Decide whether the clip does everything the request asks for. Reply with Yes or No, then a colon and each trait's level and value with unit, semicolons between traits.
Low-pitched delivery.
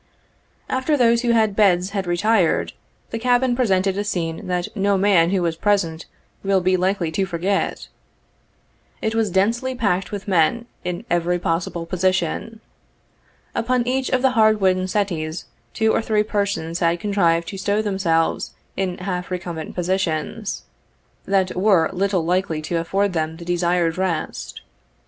No: high, 190 Hz